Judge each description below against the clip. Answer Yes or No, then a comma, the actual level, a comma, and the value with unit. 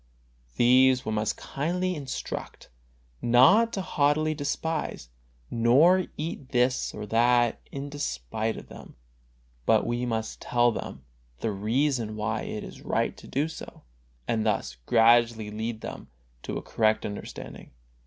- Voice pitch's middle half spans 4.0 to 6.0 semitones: Yes, average, 4.6 semitones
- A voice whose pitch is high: No, low, 120 Hz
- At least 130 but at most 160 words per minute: Yes, slow, 135 wpm